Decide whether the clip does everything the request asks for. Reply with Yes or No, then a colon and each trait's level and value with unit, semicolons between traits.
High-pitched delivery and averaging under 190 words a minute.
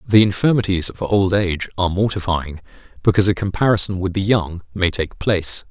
No: very low, 95 Hz; average, 170 wpm